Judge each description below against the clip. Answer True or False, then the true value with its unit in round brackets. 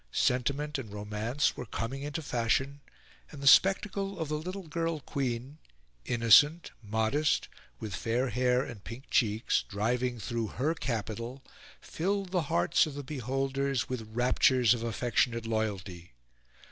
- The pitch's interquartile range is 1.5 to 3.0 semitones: False (4.3 semitones)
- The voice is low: True (125 Hz)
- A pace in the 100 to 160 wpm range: True (135 wpm)